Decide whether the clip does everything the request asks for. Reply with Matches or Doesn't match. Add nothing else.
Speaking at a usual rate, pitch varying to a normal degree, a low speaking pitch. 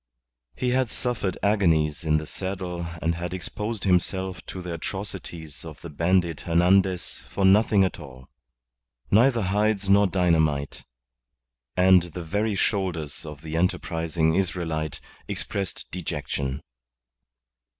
Doesn't match